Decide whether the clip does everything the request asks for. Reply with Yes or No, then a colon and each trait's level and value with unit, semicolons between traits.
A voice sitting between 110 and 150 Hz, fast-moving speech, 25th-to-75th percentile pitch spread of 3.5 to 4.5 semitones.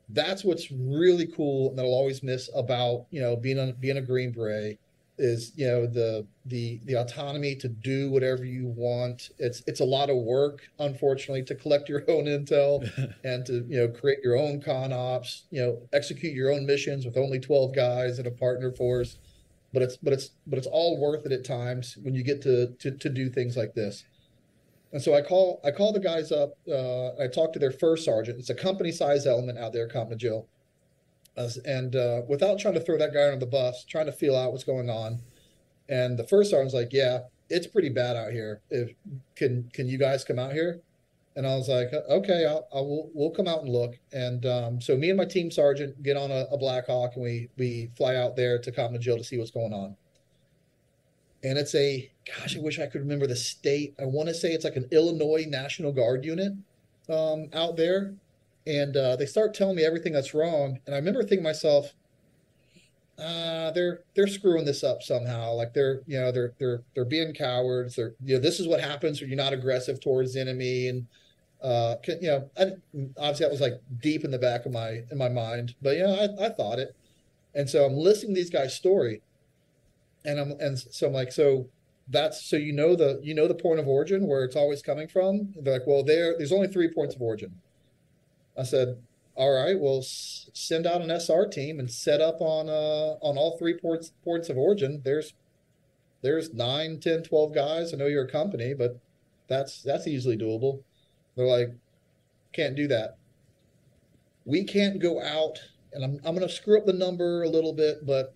Yes: medium, 140 Hz; fast, 210 wpm; average, 3.8 semitones